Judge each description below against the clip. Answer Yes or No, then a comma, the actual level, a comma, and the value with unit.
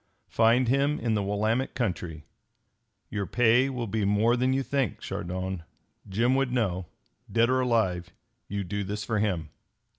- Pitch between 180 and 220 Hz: No, low, 110 Hz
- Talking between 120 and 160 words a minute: Yes, average, 155 wpm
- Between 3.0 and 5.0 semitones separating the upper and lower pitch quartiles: Yes, average, 4.3 semitones